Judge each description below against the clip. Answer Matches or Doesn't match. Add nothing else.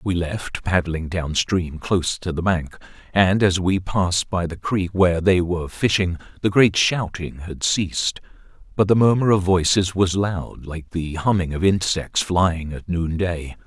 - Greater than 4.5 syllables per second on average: Doesn't match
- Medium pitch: Doesn't match